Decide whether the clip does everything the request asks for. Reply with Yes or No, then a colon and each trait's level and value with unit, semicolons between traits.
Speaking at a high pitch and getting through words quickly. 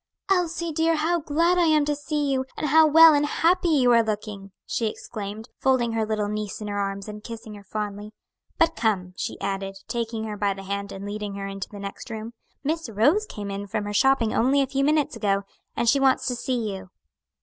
Yes: high, 225 Hz; fast, 220 wpm